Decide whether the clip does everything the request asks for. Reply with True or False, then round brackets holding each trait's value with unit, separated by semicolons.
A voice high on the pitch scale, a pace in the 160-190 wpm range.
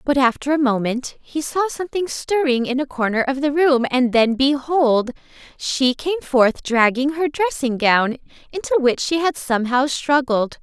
True (270 Hz; 170 wpm)